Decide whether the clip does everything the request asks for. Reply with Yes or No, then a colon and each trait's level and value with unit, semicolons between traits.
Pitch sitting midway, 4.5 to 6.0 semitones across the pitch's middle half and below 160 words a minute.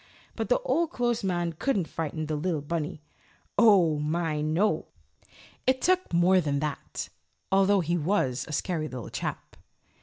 Yes: medium, 170 Hz; average, 4.8 semitones; average, 150 wpm